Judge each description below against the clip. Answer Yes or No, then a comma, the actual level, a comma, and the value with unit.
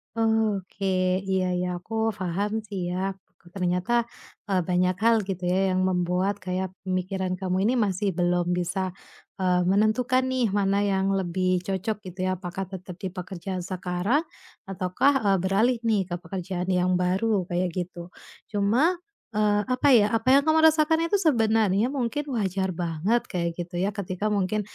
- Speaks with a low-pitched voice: No, high, 190 Hz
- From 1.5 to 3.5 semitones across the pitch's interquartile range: Yes, average, 3.1 semitones